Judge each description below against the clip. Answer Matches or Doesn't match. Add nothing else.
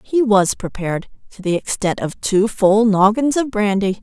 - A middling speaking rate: Matches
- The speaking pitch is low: Doesn't match